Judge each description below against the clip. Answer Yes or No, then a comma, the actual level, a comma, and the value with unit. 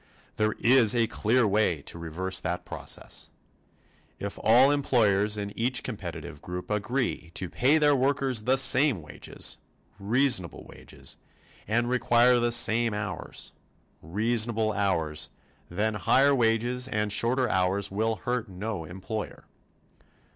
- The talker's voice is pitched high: No, low, 110 Hz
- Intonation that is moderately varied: Yes, average, 4.1 semitones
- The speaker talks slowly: Yes, slow, 125 wpm